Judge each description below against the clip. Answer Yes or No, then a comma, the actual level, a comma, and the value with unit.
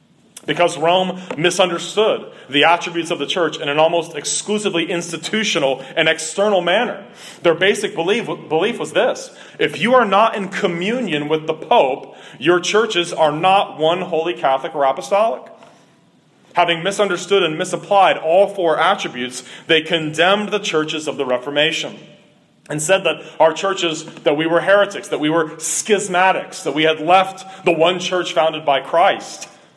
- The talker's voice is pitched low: No, medium, 170 Hz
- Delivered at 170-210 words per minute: No, average, 155 wpm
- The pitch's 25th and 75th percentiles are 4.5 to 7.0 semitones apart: No, average, 3.3 semitones